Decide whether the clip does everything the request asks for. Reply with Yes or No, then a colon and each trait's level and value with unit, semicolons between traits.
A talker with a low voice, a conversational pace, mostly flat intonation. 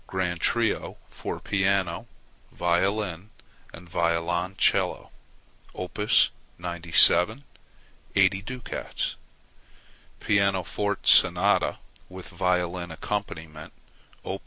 No: very low, 90 Hz; slow, 70 wpm; narrow, 2.2 semitones